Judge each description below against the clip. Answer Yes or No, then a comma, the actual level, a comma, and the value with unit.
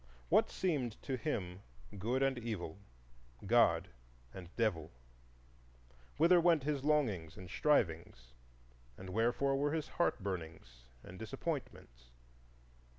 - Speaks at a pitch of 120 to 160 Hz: No, low, 110 Hz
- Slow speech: Yes, slow, 105 wpm